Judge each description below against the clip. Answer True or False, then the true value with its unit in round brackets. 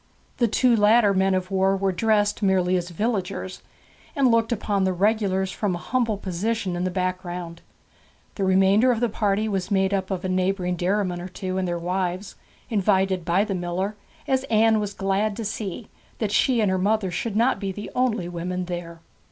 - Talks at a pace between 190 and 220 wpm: True (195 wpm)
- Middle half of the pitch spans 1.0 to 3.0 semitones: True (2.7 semitones)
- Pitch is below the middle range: False (195 Hz)